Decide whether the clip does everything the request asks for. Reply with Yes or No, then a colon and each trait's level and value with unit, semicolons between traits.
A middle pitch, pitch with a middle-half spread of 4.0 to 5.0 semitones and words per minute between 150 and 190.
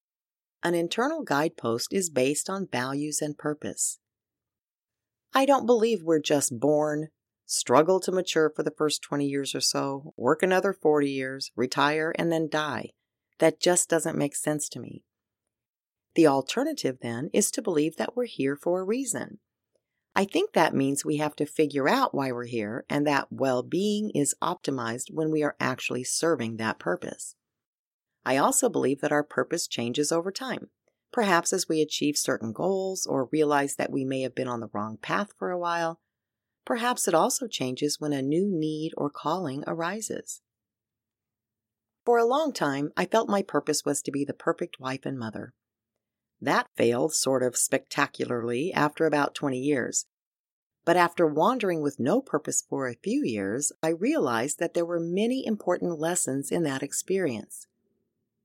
Yes: medium, 150 Hz; average, 4.5 semitones; average, 165 wpm